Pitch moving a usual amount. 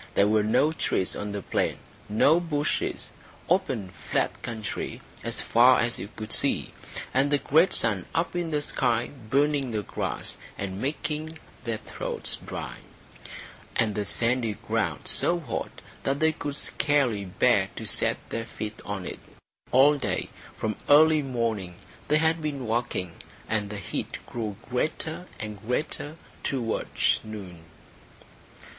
No: wide, 5.7 semitones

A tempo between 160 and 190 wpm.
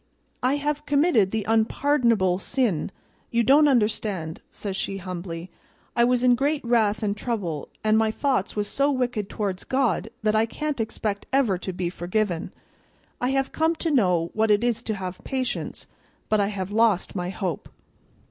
Yes: average, 170 wpm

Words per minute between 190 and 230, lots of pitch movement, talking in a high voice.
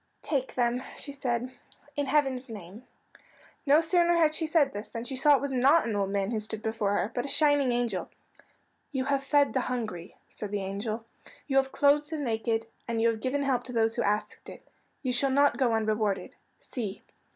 No: fast, 205 wpm; average, 4.3 semitones; very high, 250 Hz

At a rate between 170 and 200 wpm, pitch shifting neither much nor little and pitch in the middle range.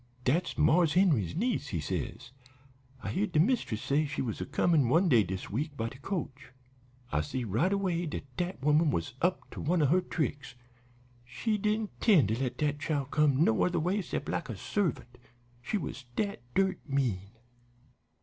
No: average, 185 wpm; wide, 6.2 semitones; medium, 150 Hz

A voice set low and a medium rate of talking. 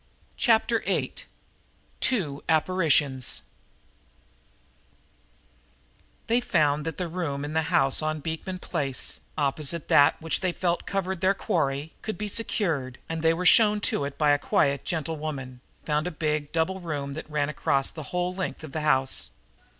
No: medium, 155 Hz; average, 155 wpm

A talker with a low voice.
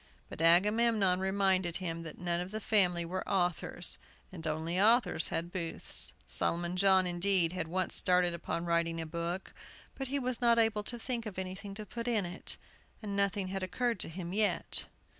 No: medium, 185 Hz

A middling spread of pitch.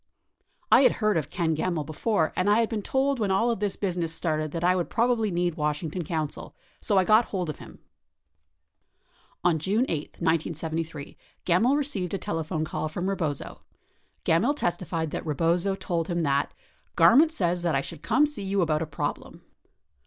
Yes: average, 4.2 semitones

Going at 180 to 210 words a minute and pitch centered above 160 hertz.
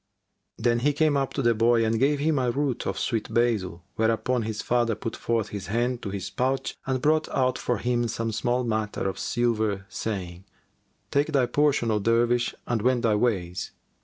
No: average, 195 wpm; low, 120 Hz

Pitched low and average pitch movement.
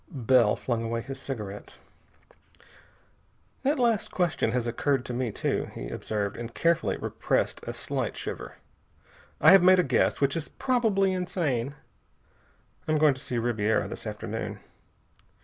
No: low, 130 Hz; wide, 7.5 semitones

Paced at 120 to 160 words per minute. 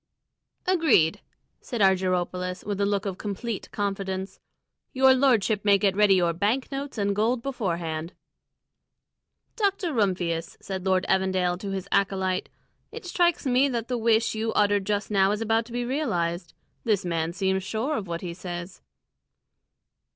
Yes: average, 150 wpm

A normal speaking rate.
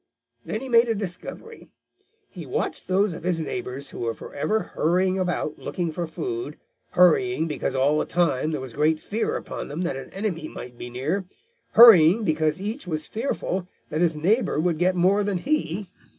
Yes: average, 180 wpm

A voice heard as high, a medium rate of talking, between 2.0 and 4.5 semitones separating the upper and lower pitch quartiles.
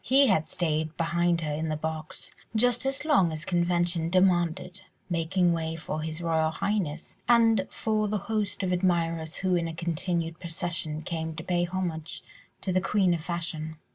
No: medium, 170 Hz; average, 170 wpm; average, 2.7 semitones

